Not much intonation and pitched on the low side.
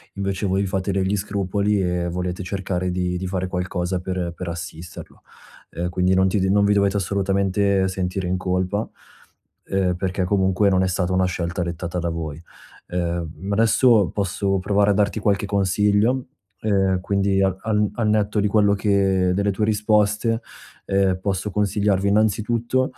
Yes: narrow, 1.9 semitones; very low, 95 Hz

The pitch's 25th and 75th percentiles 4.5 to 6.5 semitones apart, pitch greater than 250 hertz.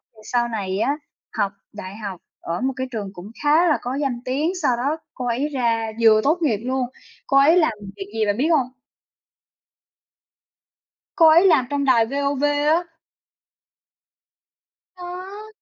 Yes: average, 5.1 semitones; very high, 260 Hz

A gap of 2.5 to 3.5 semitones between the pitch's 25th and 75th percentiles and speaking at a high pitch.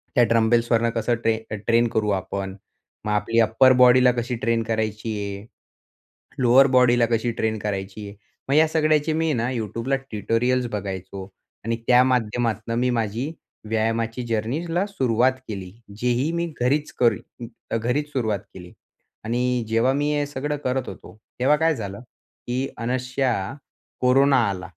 No: average, 2.8 semitones; low, 120 Hz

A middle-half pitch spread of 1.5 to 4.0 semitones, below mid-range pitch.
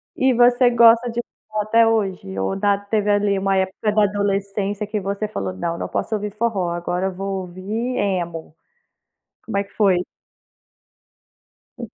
No: narrow, 2.5 semitones; high, 200 Hz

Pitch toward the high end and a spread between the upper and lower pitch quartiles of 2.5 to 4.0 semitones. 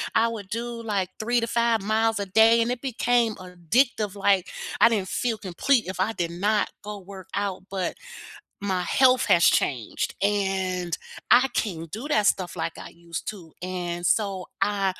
Yes: high, 200 Hz; average, 3.7 semitones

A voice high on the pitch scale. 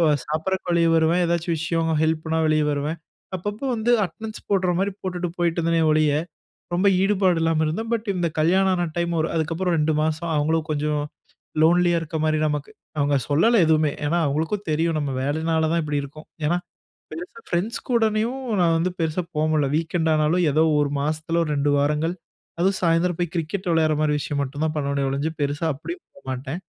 No: medium, 165 Hz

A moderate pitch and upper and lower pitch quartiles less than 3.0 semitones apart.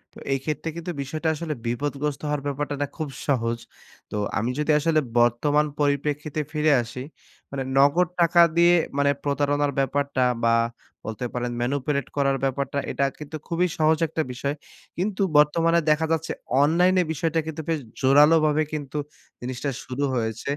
Yes: medium, 145 Hz; narrow, 2.5 semitones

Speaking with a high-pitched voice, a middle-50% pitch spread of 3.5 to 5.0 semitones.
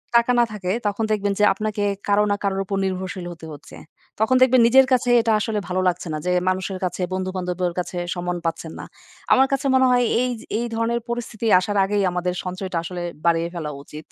Yes: high, 195 Hz; average, 4.1 semitones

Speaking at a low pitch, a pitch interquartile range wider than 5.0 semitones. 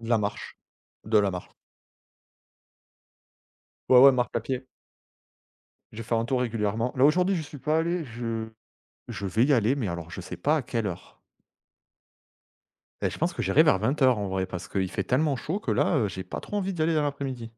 Yes: low, 120 Hz; wide, 5.6 semitones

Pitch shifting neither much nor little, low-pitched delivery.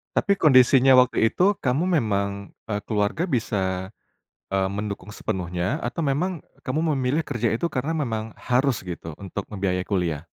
No: wide, 5.9 semitones; low, 110 Hz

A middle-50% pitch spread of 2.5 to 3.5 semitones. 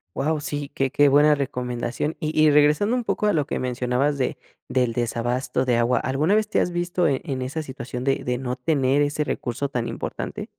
Yes: average, 3.2 semitones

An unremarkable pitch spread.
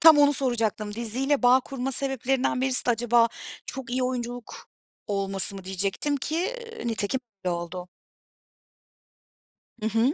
Yes: average, 4.0 semitones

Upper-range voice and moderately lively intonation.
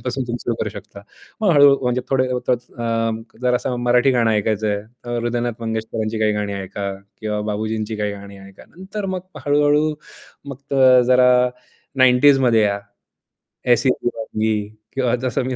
No: low, 120 Hz; average, 3.2 semitones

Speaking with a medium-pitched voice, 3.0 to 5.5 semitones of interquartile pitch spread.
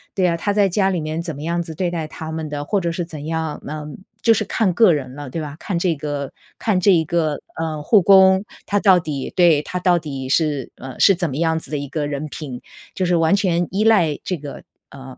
Yes: medium, 165 Hz; average, 3.6 semitones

